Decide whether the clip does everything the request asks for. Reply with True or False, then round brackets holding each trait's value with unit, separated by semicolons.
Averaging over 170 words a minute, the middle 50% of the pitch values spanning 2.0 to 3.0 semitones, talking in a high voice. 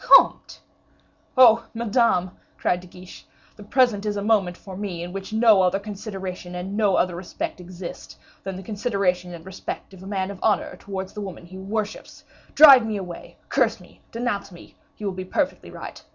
True (185 wpm; 2.7 semitones; 195 Hz)